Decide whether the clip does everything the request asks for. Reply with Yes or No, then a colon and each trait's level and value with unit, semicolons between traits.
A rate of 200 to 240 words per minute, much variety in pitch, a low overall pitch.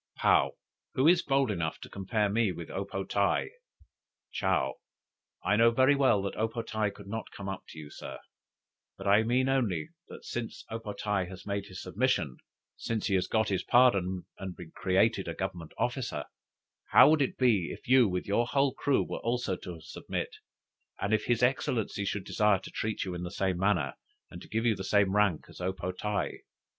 No: fast, 205 wpm; average, 3.8 semitones; low, 105 Hz